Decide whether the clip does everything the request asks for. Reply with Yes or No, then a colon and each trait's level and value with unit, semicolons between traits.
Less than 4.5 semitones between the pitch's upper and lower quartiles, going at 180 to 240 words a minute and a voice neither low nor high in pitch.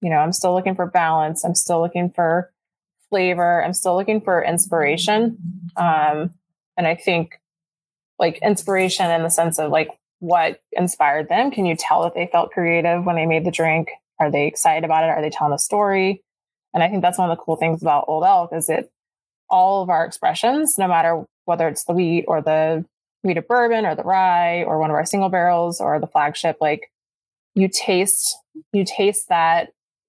Yes: narrow, 2.5 semitones; average, 200 wpm; medium, 170 Hz